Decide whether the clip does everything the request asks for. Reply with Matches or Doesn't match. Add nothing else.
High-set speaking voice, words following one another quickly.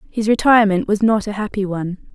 Doesn't match